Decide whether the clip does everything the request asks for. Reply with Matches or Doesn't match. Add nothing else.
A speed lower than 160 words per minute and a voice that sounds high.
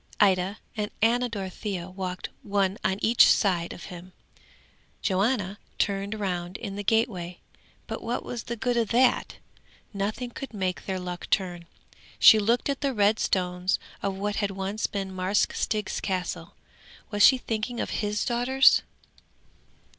Matches